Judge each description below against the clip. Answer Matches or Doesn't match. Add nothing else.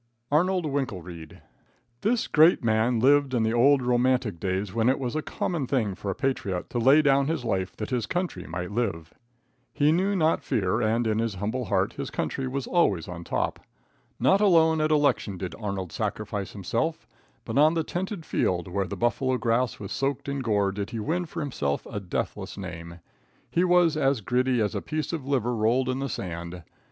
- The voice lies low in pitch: Matches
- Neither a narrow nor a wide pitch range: Doesn't match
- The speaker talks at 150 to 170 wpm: Doesn't match